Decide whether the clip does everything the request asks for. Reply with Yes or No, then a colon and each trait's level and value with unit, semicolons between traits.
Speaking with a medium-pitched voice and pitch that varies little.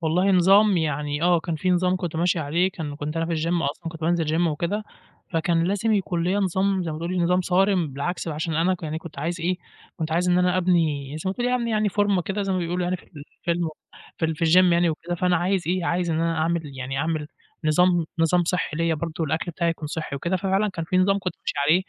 Yes: medium, 170 Hz; narrow, 2.3 semitones